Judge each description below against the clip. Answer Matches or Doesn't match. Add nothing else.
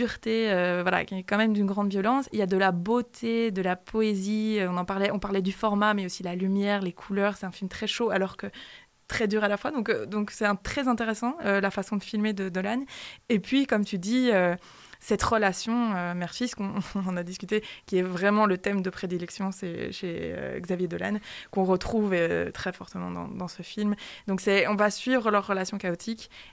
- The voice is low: Doesn't match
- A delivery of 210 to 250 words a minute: Matches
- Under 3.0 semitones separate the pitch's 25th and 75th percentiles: Matches